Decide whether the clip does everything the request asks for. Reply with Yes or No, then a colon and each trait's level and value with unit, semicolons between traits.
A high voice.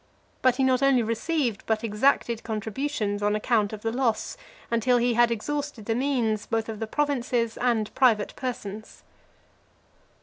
Yes: high, 230 Hz